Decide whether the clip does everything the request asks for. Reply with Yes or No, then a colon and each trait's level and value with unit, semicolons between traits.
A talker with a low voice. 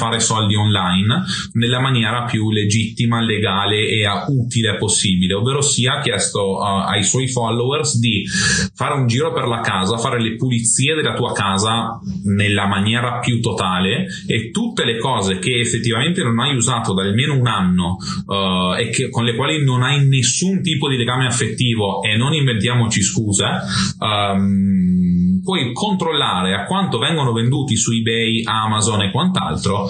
Yes: low, 115 Hz